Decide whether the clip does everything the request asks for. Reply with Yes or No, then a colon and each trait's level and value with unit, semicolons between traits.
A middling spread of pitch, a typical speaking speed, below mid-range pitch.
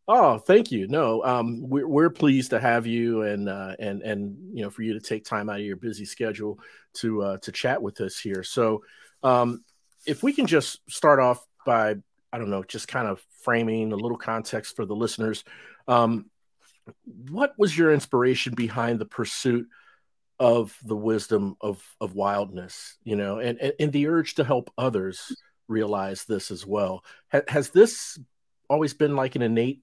Yes: average, 3.3 semitones; average, 185 wpm; low, 115 Hz